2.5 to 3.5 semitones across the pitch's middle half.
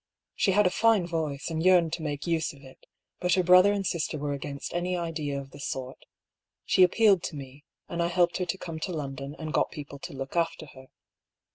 No: average, 4.0 semitones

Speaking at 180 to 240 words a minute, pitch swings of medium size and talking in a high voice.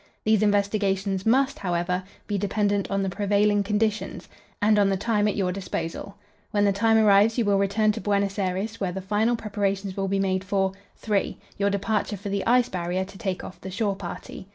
No: average, 200 wpm; narrow, 1.5 semitones; high, 200 Hz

